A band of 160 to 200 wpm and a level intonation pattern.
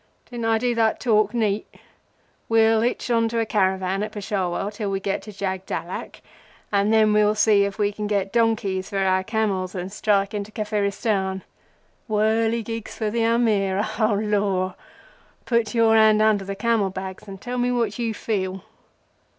Yes: average, 165 wpm; narrow, 2.3 semitones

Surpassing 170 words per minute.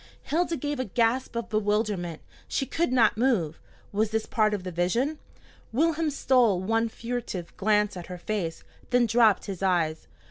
No: average, 165 wpm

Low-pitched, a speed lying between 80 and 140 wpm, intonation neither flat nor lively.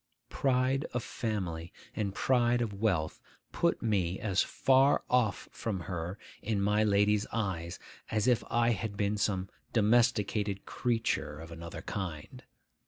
Yes: low, 105 Hz; slow, 135 wpm; average, 3.8 semitones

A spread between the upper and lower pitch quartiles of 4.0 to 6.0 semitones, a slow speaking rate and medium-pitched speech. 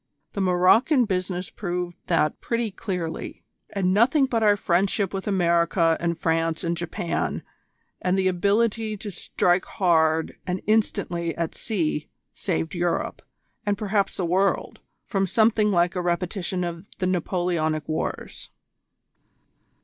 No: average, 2.9 semitones; slow, 130 wpm; medium, 180 Hz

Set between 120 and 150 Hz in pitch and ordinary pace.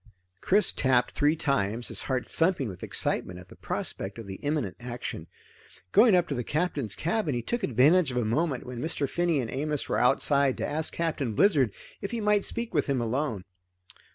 Yes: medium, 140 Hz; average, 195 wpm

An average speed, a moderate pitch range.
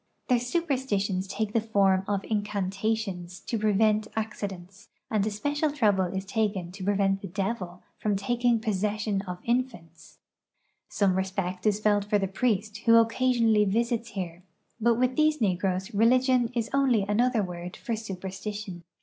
Yes: average, 150 wpm; average, 3.1 semitones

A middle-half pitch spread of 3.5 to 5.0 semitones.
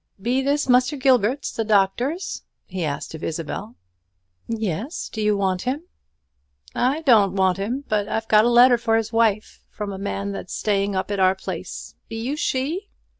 Yes: average, 4.5 semitones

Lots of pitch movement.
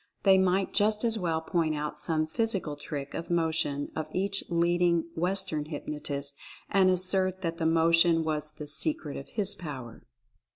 No: average, 3.7 semitones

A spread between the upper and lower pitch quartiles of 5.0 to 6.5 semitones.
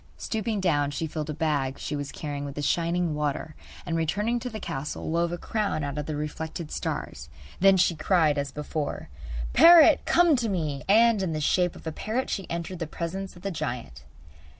No: average, 4.6 semitones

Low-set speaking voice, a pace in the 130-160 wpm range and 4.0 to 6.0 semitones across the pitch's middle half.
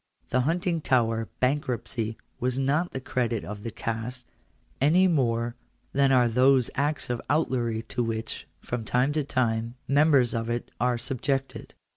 No: low, 125 Hz; average, 155 wpm; average, 3.0 semitones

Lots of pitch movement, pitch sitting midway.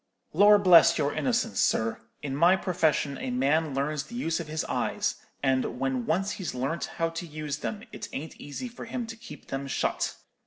Yes: wide, 5.8 semitones; medium, 160 Hz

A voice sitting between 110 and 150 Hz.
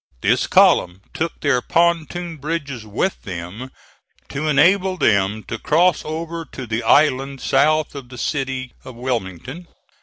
Yes: medium, 140 Hz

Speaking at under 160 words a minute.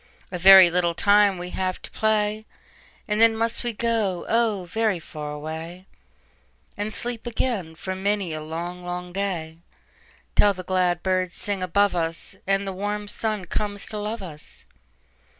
Yes: average, 140 wpm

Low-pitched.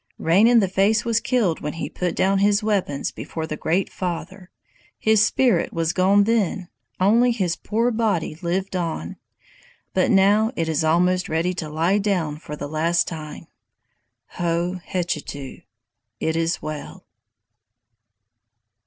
No: medium, 180 Hz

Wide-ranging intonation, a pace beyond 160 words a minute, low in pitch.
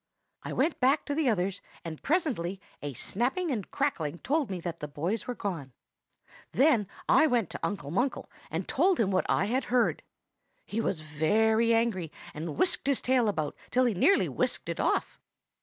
No: wide, 7.2 semitones; average, 180 wpm; high, 220 Hz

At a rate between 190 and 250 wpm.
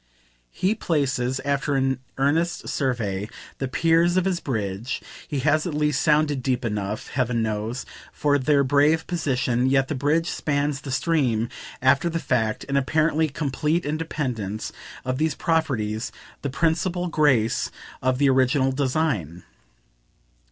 No: slow, 135 wpm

